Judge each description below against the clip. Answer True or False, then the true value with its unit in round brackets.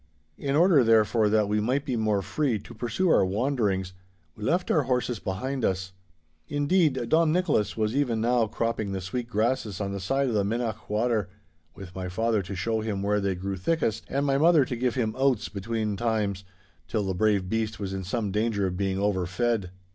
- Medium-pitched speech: False (110 Hz)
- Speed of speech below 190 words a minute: False (200 wpm)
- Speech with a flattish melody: False (4.2 semitones)